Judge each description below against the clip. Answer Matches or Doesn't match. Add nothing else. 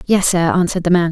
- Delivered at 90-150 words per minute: Doesn't match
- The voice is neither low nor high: Matches